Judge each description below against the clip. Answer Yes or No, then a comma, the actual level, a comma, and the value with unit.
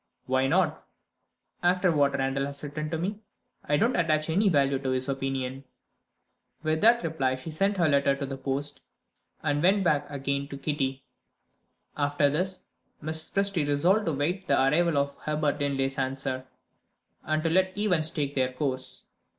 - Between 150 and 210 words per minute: Yes, average, 165 wpm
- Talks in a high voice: No, medium, 145 Hz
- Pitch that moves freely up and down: No, average, 3.4 semitones